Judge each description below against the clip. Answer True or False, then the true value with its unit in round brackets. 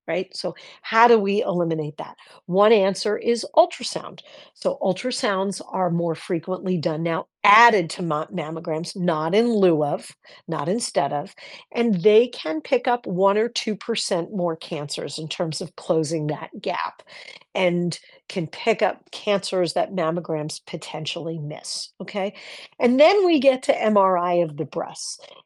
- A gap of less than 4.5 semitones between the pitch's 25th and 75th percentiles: False (4.8 semitones)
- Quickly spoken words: False (155 wpm)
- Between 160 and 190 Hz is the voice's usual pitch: True (185 Hz)